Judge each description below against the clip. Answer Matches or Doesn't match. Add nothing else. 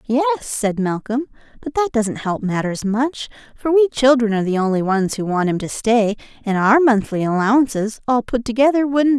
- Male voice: Doesn't match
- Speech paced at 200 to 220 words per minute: Matches